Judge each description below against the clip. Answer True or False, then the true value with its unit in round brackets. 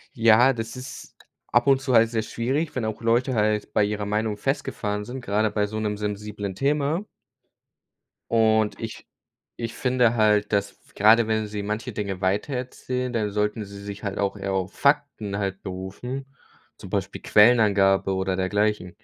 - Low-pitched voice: True (110 Hz)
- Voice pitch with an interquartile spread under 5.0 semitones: True (2.9 semitones)